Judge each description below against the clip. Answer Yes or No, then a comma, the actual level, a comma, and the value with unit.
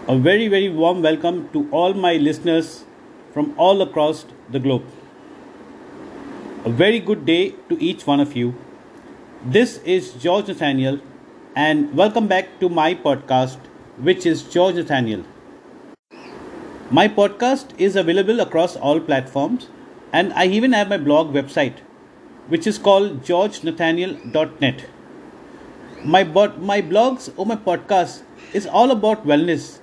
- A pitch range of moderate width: No, wide, 5.9 semitones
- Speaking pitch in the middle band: Yes, medium, 180 Hz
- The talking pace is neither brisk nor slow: No, slow, 130 wpm